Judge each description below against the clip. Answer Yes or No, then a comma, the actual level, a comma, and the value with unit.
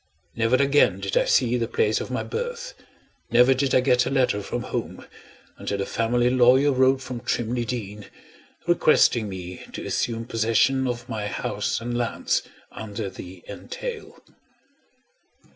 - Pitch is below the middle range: Yes, low, 120 Hz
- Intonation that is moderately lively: Yes, average, 3.1 semitones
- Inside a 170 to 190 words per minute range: No, average, 150 wpm